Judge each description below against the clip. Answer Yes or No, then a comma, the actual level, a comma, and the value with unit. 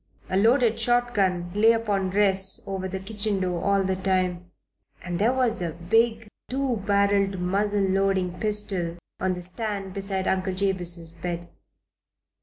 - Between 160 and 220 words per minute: No, average, 145 wpm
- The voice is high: Yes, high, 195 Hz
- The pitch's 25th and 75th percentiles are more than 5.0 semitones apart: No, narrow, 2.4 semitones